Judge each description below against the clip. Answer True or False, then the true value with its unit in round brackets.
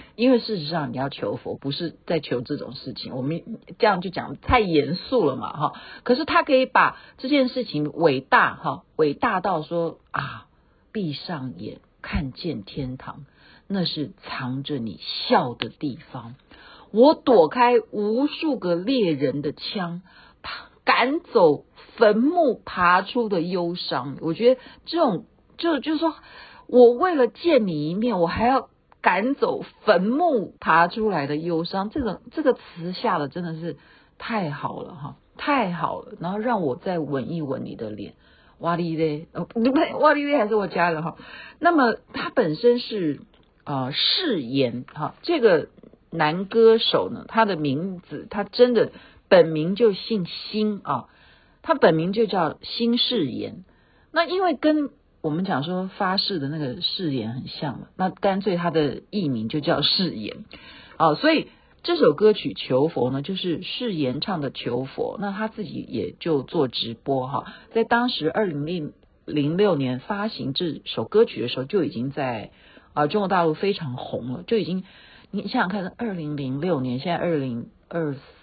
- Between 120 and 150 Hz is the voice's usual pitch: False (185 Hz)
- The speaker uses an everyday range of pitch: False (7.8 semitones)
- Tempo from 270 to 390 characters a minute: False (225 characters per minute)